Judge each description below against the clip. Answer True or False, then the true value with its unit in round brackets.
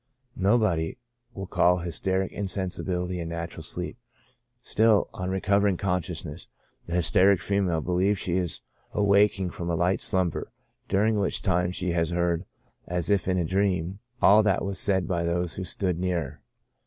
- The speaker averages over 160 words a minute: False (155 wpm)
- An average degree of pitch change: False (2.1 semitones)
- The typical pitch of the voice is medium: False (90 Hz)